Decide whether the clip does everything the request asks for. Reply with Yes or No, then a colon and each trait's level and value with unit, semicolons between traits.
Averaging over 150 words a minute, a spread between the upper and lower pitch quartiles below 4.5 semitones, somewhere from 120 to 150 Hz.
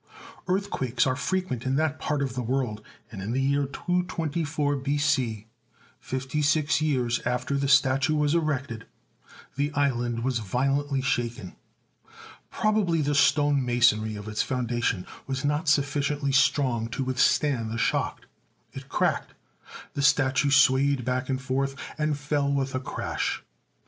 No: average, 145 wpm; average, 2.7 semitones; low, 135 Hz